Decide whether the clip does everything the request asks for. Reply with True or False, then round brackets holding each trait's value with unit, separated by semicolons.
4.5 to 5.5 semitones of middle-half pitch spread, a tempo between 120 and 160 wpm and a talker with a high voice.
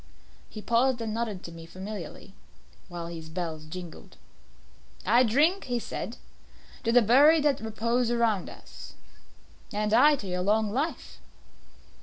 True (5.1 semitones; 140 wpm; 220 Hz)